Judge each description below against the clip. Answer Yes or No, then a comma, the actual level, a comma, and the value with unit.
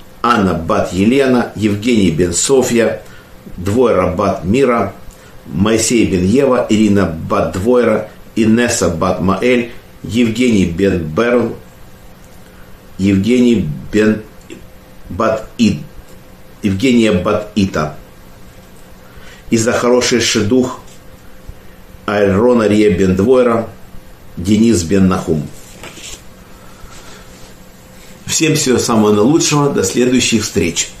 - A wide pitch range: No, average, 4.0 semitones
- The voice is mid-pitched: No, low, 110 Hz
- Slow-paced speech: Yes, slow, 70 wpm